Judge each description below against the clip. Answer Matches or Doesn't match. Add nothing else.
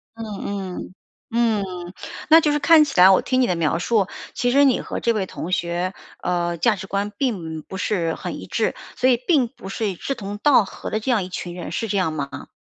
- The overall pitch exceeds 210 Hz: Doesn't match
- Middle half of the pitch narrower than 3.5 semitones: Doesn't match